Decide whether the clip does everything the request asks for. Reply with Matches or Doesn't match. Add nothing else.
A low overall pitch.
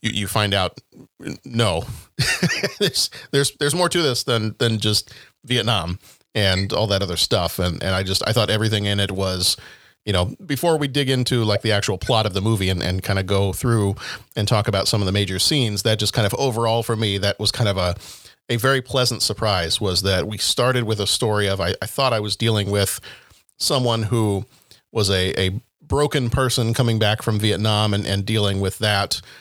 Matches